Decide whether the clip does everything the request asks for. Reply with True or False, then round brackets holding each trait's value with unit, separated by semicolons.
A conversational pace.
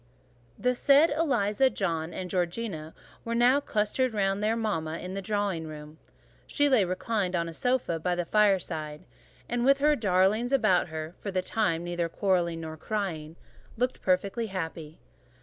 True (160 wpm)